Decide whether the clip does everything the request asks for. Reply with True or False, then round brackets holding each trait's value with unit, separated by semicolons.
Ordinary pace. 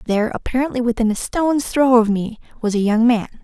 True (175 wpm)